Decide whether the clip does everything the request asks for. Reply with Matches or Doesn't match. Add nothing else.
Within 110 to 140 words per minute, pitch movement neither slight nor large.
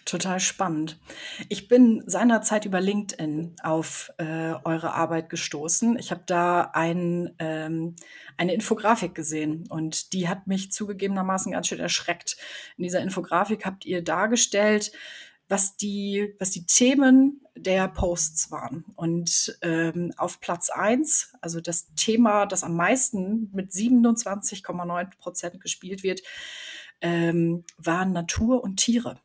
Matches